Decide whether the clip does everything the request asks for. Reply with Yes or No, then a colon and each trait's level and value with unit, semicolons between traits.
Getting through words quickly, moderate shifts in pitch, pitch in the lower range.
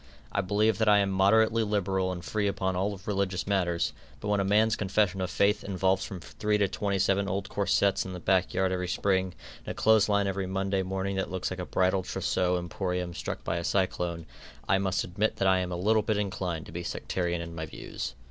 No: fast, 225 wpm; narrow, 1.7 semitones; very low, 95 Hz